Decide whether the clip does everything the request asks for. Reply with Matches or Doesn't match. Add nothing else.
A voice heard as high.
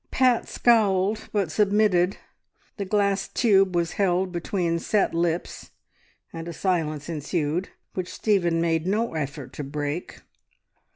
Doesn't match